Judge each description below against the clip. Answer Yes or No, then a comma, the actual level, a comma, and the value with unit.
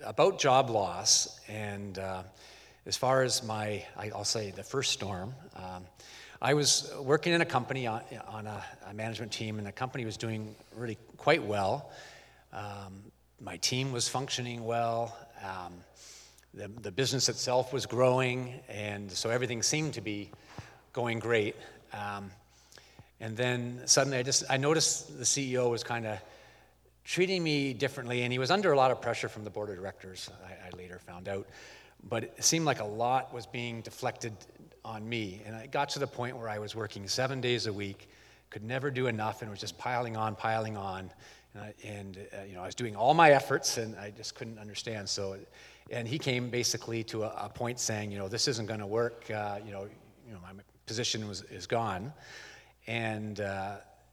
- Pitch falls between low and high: No, low, 115 Hz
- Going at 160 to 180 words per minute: No, average, 190 wpm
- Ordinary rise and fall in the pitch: Yes, average, 3.6 semitones